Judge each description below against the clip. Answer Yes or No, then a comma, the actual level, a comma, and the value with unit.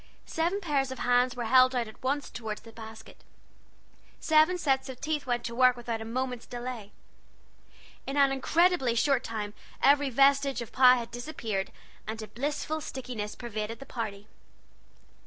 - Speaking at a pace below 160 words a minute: No, average, 165 wpm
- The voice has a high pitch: Yes, very high, 250 Hz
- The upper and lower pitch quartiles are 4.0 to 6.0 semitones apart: No, average, 3.3 semitones